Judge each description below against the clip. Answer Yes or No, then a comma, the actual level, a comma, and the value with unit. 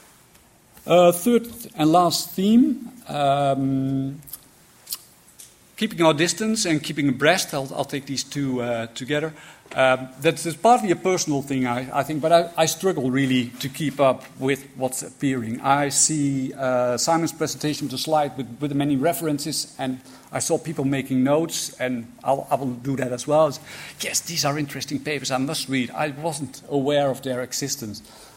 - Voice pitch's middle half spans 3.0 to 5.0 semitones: Yes, average, 3.3 semitones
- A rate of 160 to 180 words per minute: Yes, average, 170 wpm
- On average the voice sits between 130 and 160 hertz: Yes, medium, 140 Hz